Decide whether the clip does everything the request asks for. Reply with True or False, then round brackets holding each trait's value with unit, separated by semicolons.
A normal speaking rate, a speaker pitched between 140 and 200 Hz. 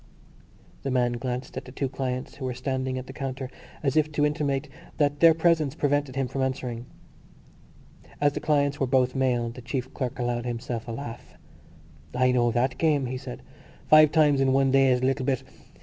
False (195 wpm; 130 Hz)